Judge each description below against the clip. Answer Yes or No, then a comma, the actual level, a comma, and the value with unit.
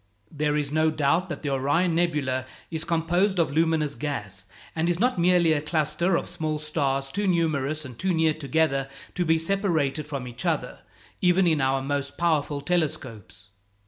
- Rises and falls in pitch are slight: No, average, 3.3 semitones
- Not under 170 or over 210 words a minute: Yes, average, 175 wpm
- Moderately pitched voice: Yes, medium, 155 Hz